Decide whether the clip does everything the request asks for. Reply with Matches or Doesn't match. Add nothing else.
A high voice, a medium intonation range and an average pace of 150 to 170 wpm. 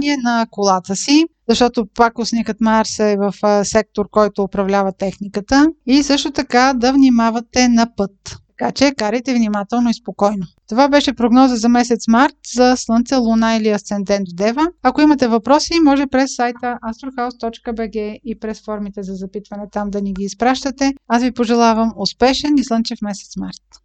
Matches